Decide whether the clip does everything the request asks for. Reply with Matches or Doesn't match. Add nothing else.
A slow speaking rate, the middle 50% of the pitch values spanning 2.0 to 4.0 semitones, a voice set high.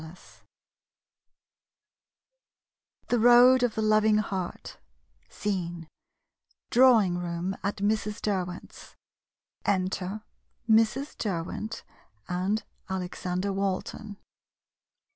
Matches